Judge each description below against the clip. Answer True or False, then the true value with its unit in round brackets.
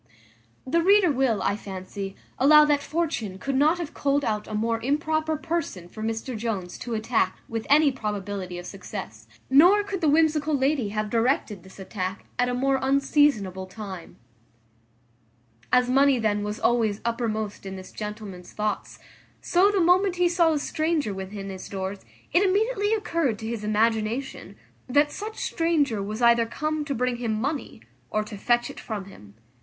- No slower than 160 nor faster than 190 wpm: True (170 wpm)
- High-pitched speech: True (235 Hz)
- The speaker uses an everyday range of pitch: False (6.4 semitones)